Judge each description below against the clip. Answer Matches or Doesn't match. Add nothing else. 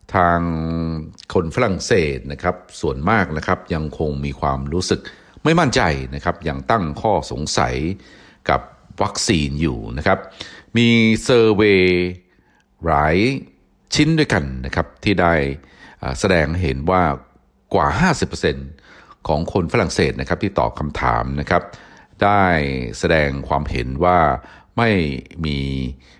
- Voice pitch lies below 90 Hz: Matches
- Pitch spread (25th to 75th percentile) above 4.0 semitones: Matches